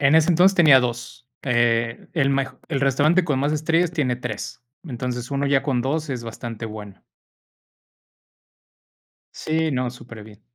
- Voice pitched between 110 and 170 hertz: Yes, low, 135 Hz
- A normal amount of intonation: Yes, average, 4.3 semitones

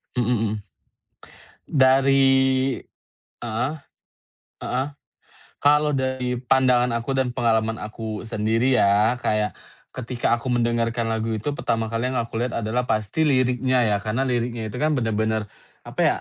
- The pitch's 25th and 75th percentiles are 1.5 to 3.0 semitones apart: Yes, average, 2.7 semitones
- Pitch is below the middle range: Yes, low, 120 Hz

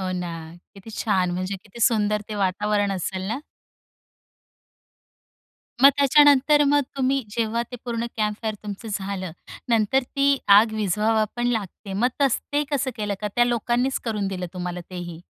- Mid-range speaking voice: No, high, 215 Hz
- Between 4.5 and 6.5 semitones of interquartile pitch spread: No, average, 3.9 semitones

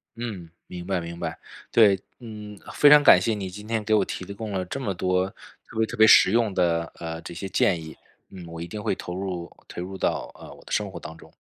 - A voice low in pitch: Yes, very low, 95 Hz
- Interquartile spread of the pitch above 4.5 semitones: No, average, 3.7 semitones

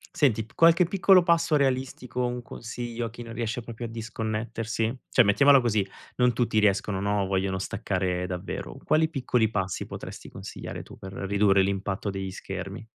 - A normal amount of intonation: Yes, average, 4.0 semitones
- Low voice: Yes, low, 115 Hz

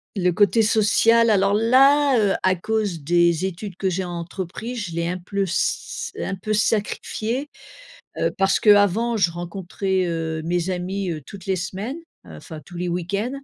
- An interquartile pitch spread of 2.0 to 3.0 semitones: No, average, 3.6 semitones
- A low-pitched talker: No, high, 190 Hz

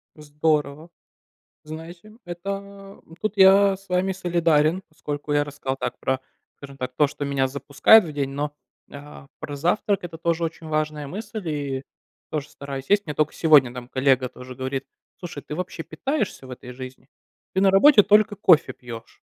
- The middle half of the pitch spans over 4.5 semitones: Yes, average, 5.1 semitones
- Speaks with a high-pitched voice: No, medium, 155 Hz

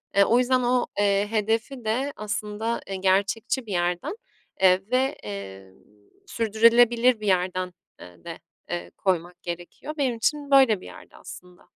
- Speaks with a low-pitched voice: No, high, 210 Hz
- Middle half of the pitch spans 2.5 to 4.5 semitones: No, average, 4.9 semitones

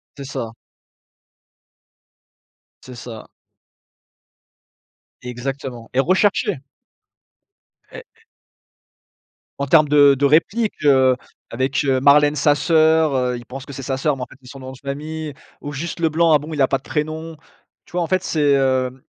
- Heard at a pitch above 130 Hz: Yes, medium, 140 Hz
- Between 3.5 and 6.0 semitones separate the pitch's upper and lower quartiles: No, average, 3.1 semitones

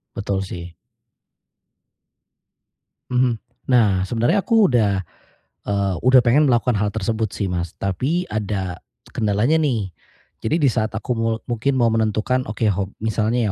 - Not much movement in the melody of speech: No, average, 3.7 semitones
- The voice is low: Yes, low, 110 Hz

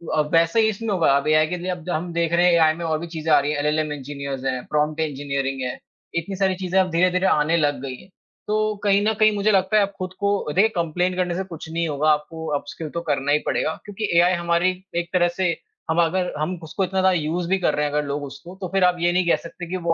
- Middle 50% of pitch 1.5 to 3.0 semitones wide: No, average, 3.4 semitones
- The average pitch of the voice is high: No, medium, 170 Hz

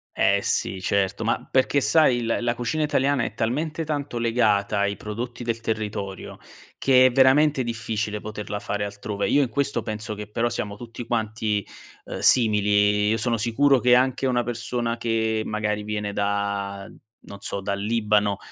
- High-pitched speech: No, low, 110 Hz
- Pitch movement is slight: No, average, 3.0 semitones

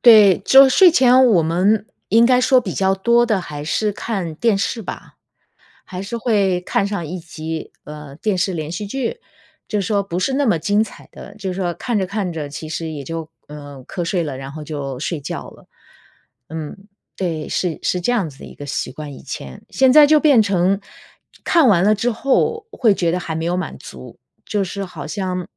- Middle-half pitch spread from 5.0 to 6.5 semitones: Yes, average, 5.3 semitones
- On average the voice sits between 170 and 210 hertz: Yes, high, 190 Hz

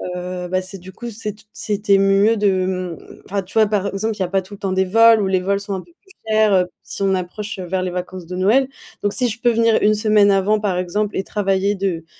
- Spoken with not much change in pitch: Yes, narrow, 2.3 semitones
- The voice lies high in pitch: Yes, high, 195 Hz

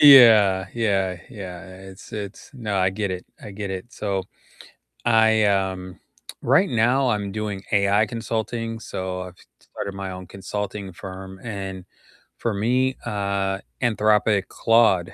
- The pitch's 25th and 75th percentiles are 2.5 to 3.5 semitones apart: Yes, average, 2.9 semitones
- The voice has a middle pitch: No, low, 100 Hz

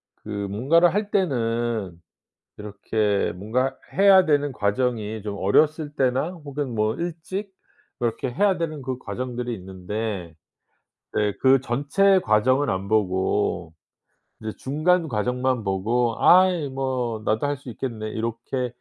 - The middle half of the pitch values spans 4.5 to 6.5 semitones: Yes, average, 5.3 semitones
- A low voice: Yes, low, 125 Hz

